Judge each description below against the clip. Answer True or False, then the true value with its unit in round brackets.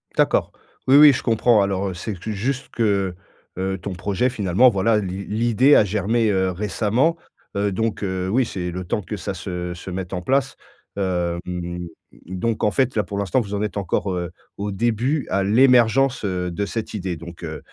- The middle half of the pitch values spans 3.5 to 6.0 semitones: True (3.9 semitones)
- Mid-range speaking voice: False (100 Hz)